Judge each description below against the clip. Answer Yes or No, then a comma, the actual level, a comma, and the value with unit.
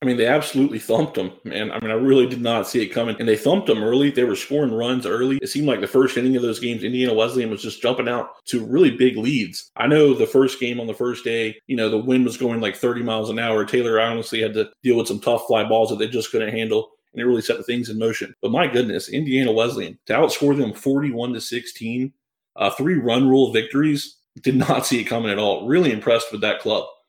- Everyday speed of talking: No, fast, 255 wpm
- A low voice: Yes, low, 125 Hz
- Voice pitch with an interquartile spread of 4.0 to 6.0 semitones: No, average, 2.9 semitones